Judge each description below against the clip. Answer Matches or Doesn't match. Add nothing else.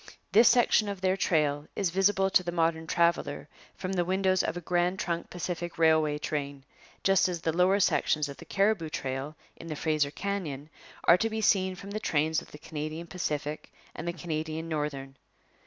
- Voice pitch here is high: Doesn't match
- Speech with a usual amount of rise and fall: Matches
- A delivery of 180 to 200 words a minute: Matches